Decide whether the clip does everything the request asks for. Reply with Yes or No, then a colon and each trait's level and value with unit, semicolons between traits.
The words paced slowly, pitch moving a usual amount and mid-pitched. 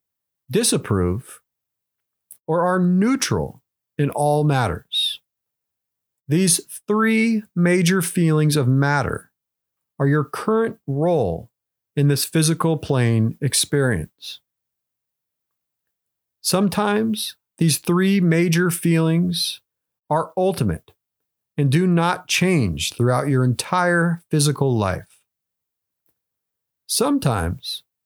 Yes: slow, 85 wpm; average, 4.8 semitones; medium, 160 Hz